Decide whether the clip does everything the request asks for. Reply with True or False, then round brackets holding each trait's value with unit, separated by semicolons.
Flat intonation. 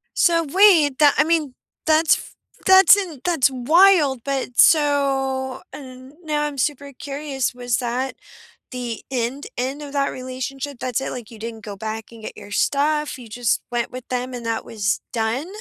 False (3.3 semitones)